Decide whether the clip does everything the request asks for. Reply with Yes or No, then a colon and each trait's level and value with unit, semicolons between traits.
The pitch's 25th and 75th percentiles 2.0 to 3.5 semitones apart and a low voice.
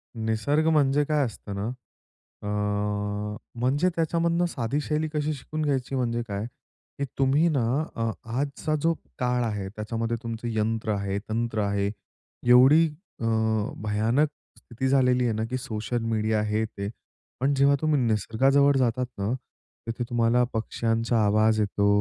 No: average, 4.2 semitones; low, 120 Hz